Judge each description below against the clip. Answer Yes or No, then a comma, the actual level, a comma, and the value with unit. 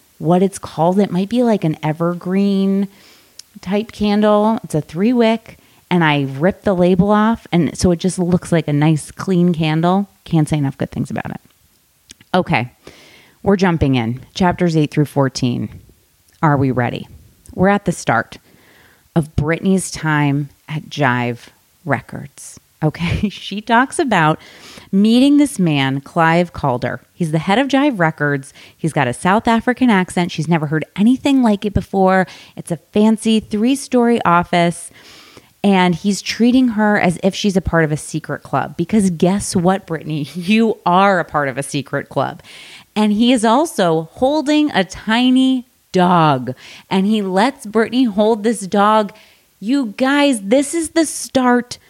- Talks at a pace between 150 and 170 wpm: Yes, average, 160 wpm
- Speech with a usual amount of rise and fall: No, wide, 5.8 semitones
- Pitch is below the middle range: No, medium, 185 Hz